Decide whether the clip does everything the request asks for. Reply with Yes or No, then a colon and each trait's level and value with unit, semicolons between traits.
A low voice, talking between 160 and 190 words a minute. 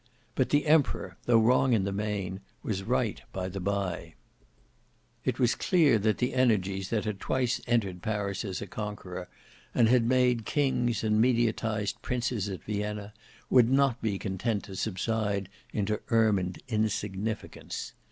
No: low, 110 Hz; average, 150 wpm